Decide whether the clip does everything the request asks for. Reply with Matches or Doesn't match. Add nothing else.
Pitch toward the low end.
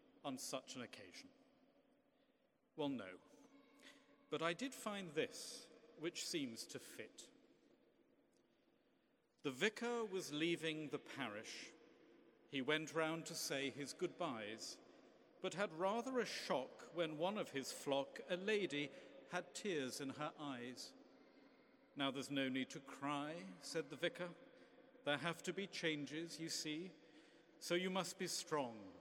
Doesn't match